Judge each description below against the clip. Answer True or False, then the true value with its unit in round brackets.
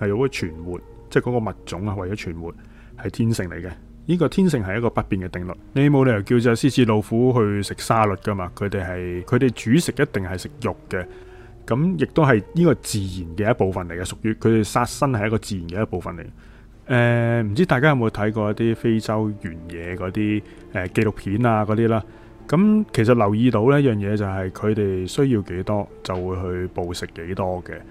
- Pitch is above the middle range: False (110 Hz)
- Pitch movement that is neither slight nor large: True (4.3 semitones)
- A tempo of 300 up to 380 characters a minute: True (320 characters per minute)